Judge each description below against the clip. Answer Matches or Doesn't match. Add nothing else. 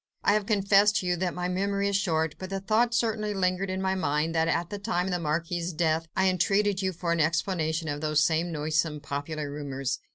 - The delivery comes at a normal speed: Doesn't match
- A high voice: Doesn't match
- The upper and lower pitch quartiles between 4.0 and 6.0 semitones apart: Doesn't match